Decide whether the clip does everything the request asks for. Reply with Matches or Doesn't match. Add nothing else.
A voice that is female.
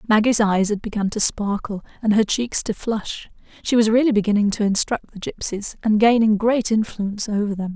Matches